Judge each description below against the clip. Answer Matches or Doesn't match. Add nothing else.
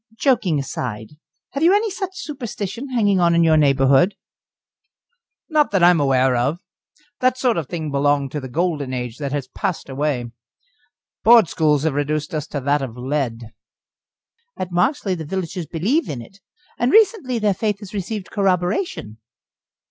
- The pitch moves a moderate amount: Doesn't match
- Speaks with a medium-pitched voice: Matches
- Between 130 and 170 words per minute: Matches